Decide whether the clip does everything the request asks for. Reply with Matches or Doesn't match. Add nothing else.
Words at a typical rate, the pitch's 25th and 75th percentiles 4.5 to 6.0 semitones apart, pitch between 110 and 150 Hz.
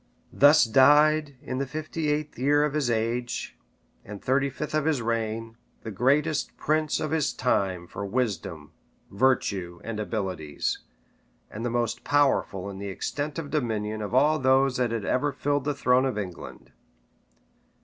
Matches